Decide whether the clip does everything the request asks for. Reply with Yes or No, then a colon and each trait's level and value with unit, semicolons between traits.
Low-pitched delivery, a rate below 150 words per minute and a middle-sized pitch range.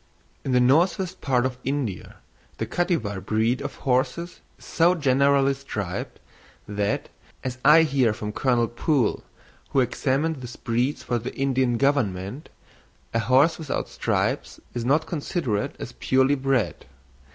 Yes: low, 130 Hz; average, 140 wpm; average, 3.3 semitones